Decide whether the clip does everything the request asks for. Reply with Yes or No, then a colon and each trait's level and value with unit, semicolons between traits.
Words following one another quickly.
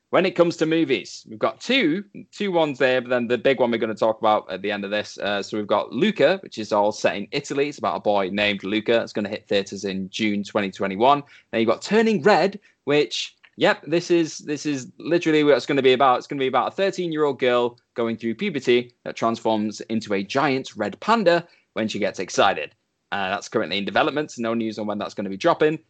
Yes: fast, 245 wpm